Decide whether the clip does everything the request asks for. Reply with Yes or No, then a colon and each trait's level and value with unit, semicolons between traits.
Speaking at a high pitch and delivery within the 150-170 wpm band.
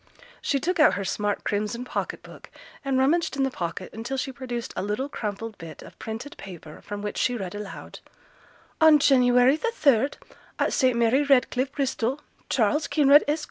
No: very high, 250 Hz; average, 180 wpm